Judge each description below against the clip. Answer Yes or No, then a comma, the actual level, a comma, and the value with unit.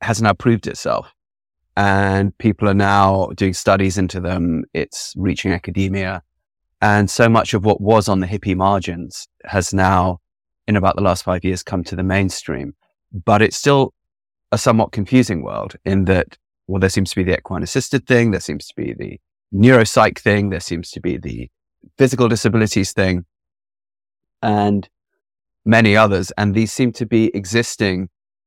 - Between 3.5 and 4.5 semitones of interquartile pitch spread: No, average, 2.8 semitones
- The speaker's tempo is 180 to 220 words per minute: No, average, 165 wpm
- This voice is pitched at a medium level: No, low, 100 Hz